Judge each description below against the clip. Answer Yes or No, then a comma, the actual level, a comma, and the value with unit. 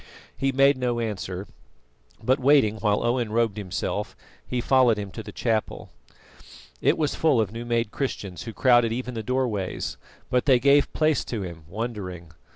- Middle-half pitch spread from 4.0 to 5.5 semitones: No, average, 3.6 semitones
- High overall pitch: No, low, 115 Hz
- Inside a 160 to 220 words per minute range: Yes, average, 165 wpm